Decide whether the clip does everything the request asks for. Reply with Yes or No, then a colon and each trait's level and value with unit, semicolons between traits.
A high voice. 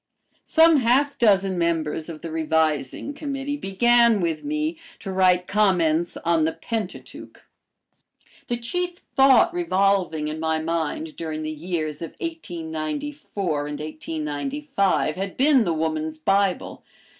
No: medium, 180 Hz